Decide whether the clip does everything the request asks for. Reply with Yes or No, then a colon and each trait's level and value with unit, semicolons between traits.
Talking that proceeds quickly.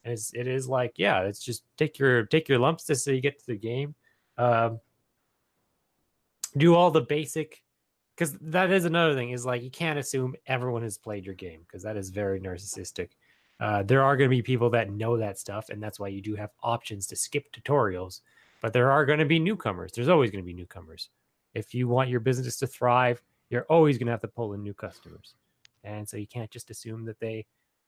Yes: fast, 225 wpm